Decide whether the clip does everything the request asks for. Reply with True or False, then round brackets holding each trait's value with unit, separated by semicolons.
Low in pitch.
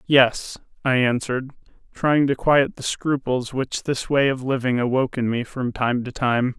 True (130 Hz)